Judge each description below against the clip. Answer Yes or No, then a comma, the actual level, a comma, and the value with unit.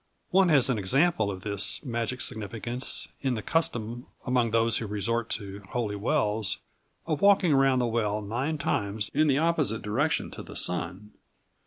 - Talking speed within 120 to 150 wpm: No, average, 165 wpm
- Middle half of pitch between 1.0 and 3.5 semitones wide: No, average, 4.6 semitones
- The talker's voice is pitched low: Yes, low, 115 Hz